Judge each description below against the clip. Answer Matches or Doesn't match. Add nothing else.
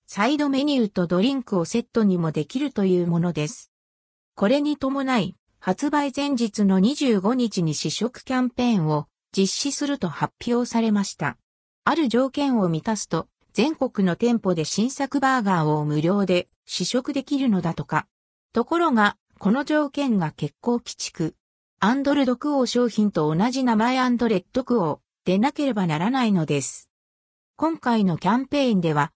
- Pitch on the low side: Doesn't match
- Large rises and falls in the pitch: Matches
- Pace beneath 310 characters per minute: Doesn't match